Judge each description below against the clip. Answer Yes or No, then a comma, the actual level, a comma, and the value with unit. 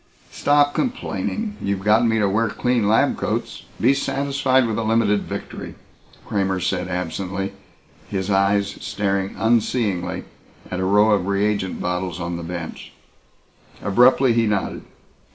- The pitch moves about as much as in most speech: Yes, average, 3.4 semitones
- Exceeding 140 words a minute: No, slow, 135 wpm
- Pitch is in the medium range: No, low, 100 Hz